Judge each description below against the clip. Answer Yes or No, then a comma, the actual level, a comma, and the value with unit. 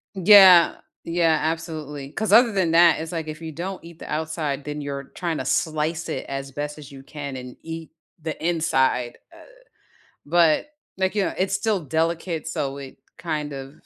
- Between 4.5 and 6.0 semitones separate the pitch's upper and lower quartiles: No, average, 2.9 semitones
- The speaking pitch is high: No, medium, 160 Hz